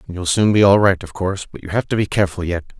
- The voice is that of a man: Yes, male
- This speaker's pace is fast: Yes, fast, 300 wpm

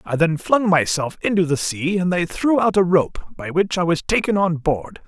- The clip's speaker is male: Yes, male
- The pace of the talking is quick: Yes, fast, 235 wpm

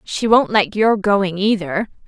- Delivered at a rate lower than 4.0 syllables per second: Yes, 3.8 syllables/s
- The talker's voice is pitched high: Yes, high, 200 Hz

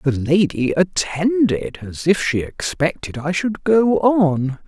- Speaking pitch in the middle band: Yes, medium, 170 Hz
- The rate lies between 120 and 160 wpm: Yes, average, 140 wpm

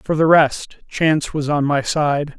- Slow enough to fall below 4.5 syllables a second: Yes, 4.0 syllables/s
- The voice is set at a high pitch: No, medium, 150 Hz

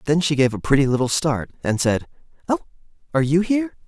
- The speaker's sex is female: No, male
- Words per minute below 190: No, average, 200 wpm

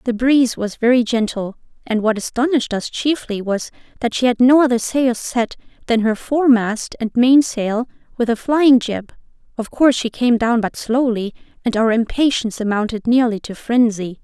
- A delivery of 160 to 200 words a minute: Yes, average, 170 wpm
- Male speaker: No, female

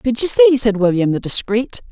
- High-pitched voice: Yes, high, 225 Hz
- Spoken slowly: No, fast, 220 wpm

